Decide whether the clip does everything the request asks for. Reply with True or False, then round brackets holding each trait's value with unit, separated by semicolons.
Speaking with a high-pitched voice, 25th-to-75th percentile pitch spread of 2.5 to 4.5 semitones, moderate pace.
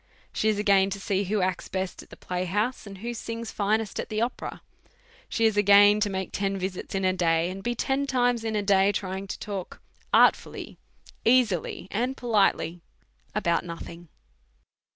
True (200 Hz; 2.9 semitones; 175 wpm)